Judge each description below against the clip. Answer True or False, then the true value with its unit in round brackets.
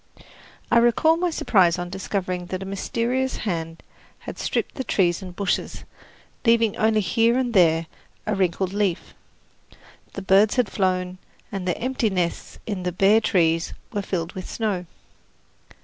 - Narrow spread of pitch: False (3.8 semitones)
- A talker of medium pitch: False (195 Hz)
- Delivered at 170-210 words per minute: False (150 wpm)